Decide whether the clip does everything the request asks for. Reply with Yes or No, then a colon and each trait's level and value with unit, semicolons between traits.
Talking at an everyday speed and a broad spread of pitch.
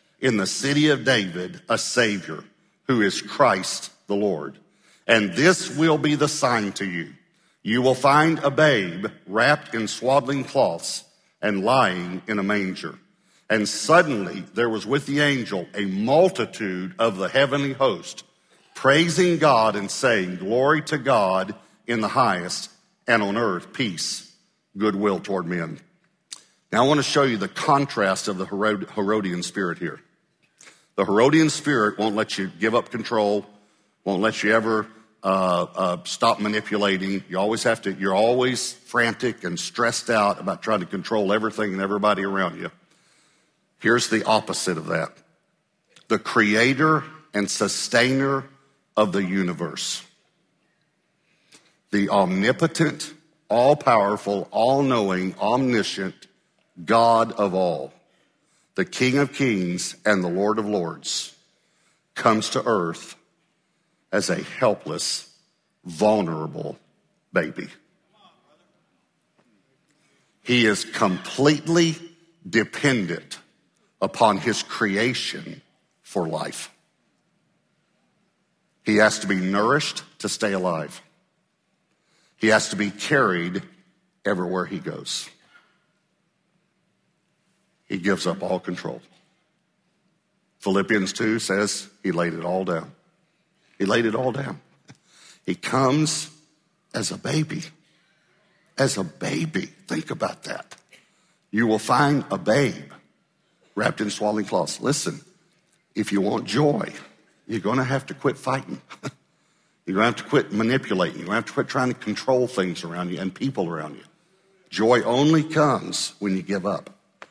No: slow, 130 wpm; wide, 7.0 semitones